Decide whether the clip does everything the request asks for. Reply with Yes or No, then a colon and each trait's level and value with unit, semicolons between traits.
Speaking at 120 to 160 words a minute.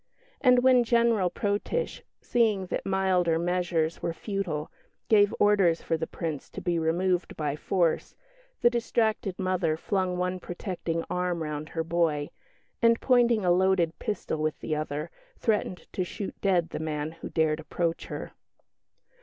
Yes: average, 150 wpm